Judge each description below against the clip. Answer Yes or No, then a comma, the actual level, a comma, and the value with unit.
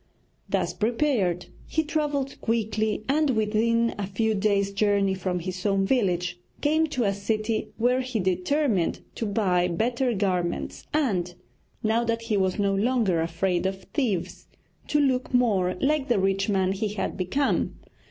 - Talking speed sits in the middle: Yes, average, 150 wpm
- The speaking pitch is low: No, high, 215 Hz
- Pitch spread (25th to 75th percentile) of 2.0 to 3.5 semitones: No, average, 4.6 semitones